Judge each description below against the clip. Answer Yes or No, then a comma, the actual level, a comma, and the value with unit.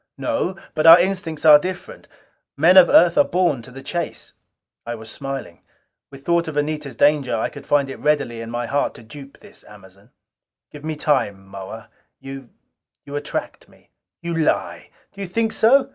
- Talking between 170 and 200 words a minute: Yes, average, 175 wpm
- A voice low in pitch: No, medium, 145 Hz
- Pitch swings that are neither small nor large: No, wide, 6.0 semitones